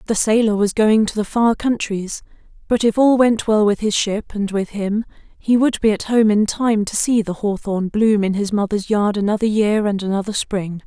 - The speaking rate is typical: No, fast, 220 wpm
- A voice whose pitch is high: Yes, high, 210 Hz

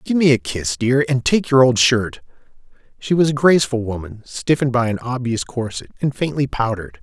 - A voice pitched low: Yes, low, 125 Hz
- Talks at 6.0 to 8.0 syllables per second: No, 5.5 syllables/s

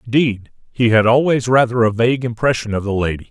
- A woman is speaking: No, male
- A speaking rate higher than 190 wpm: Yes, average, 200 wpm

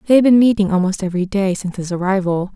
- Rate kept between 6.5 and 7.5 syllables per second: Yes, 7.2 syllables/s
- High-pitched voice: Yes, high, 195 Hz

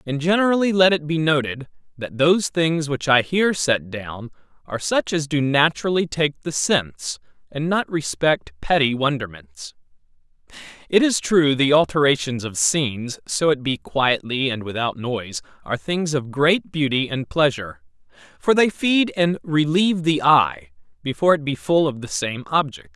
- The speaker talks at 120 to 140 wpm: No, average, 165 wpm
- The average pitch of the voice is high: No, medium, 145 Hz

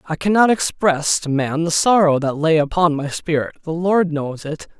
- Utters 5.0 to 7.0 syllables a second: No, 4.7 syllables/s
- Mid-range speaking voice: Yes, medium, 160 Hz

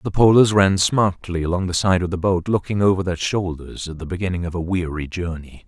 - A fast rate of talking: Yes, fast, 220 wpm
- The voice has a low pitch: Yes, very low, 90 Hz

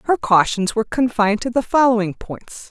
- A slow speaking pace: No, average, 175 wpm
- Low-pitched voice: No, high, 225 Hz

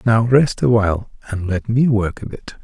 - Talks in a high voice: No, low, 110 Hz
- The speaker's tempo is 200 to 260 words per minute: Yes, fast, 205 wpm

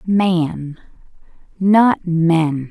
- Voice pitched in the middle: Yes, medium, 175 Hz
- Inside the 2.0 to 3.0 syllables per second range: No, 1.7 syllables/s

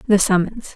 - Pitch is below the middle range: No, high, 200 Hz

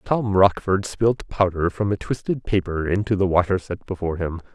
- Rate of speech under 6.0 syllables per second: Yes, 5.1 syllables/s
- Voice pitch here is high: No, very low, 95 Hz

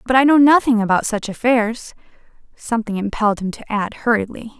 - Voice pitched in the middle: No, high, 225 Hz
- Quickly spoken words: No, average, 170 wpm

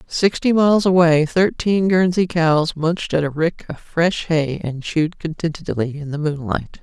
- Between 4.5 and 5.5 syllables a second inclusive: Yes, 4.6 syllables/s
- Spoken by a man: No, female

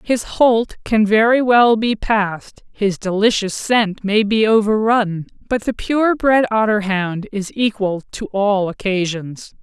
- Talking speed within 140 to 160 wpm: Yes, average, 145 wpm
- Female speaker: Yes, female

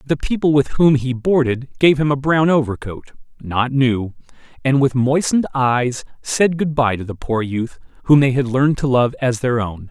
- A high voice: No, low, 130 Hz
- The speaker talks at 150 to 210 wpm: Yes, average, 200 wpm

